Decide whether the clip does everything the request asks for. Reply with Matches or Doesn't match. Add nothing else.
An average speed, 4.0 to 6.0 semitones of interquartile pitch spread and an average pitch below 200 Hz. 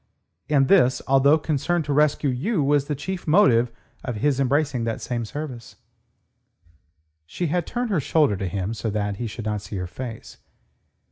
Matches